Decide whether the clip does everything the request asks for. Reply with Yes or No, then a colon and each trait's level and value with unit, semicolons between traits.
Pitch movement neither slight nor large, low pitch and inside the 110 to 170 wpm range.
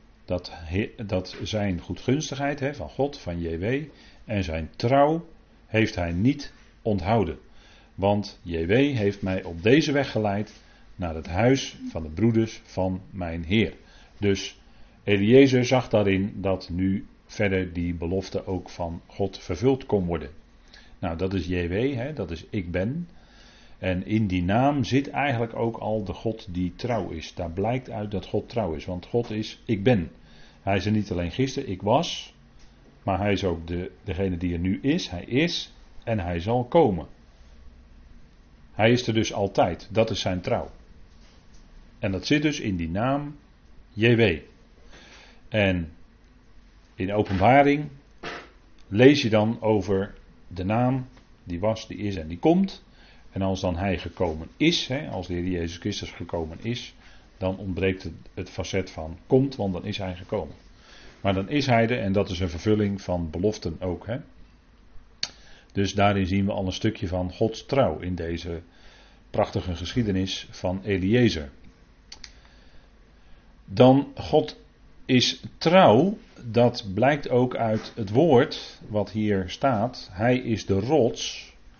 Yes: average, 4.8 semitones; low, 100 Hz; average, 155 wpm